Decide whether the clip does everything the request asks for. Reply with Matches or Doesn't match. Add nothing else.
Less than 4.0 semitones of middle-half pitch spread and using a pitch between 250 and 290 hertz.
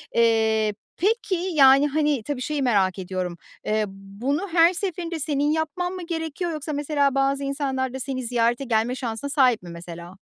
Doesn't match